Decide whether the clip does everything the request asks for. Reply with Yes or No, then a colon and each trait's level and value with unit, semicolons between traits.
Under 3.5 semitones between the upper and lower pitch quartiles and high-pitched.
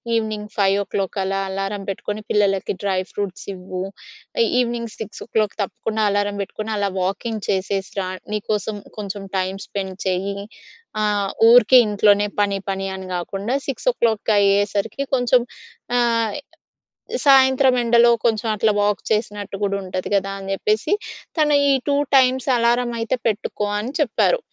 Yes: average, 2.8 semitones; high, 205 Hz